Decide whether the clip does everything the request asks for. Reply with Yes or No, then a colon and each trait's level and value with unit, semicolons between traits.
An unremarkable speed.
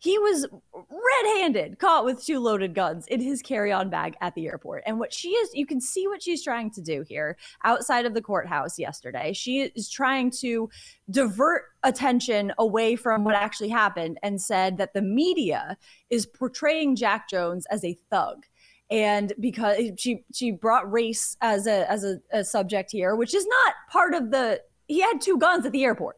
Yes: average, 190 wpm